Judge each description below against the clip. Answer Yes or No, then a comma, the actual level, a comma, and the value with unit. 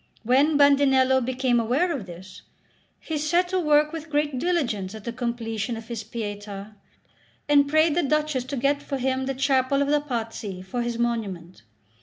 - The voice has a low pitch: No, very high, 260 Hz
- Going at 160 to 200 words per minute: Yes, average, 175 wpm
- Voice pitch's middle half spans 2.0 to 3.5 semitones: No, average, 4.5 semitones